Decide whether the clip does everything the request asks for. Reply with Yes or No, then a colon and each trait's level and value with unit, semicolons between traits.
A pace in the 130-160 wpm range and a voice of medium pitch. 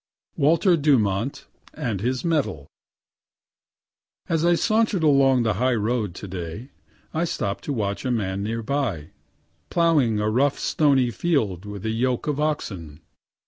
No: average, 140 wpm; low, 125 Hz